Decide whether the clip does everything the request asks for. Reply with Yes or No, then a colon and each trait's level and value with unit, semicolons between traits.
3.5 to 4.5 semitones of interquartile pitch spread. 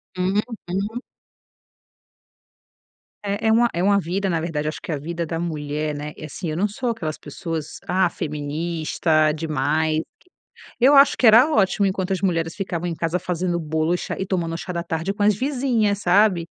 Yes: average, 4.1 semitones